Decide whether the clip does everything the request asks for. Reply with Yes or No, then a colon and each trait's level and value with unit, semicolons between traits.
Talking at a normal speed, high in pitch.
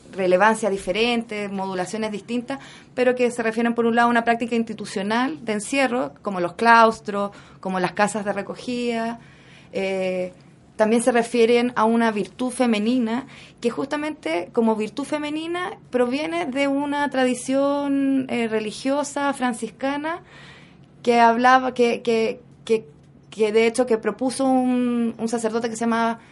Yes: average, 140 wpm; high, 235 Hz